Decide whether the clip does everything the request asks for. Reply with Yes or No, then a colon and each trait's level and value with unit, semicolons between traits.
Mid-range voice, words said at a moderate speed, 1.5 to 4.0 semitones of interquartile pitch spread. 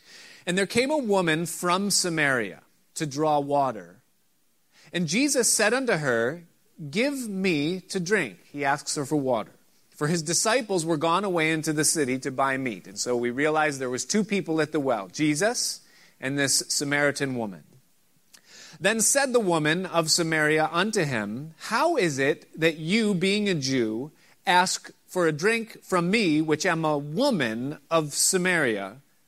No: medium, 165 Hz; average, 165 wpm; average, 5.1 semitones